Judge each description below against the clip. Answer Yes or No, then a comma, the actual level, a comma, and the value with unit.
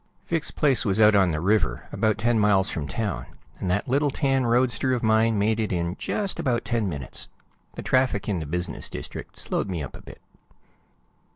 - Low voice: Yes, low, 110 Hz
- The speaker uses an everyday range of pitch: Yes, average, 4.8 semitones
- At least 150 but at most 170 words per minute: No, average, 195 wpm